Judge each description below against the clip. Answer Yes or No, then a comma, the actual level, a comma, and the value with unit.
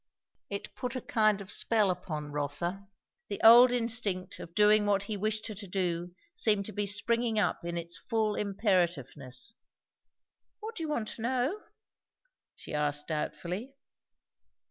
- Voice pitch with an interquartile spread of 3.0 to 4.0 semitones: No, average, 4.4 semitones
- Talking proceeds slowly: No, average, 150 wpm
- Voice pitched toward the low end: No, high, 205 Hz